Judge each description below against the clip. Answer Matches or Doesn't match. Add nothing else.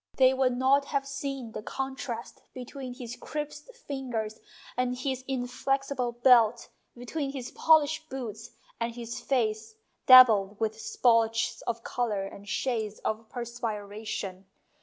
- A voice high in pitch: Matches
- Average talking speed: Doesn't match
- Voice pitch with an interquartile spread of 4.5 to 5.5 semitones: Doesn't match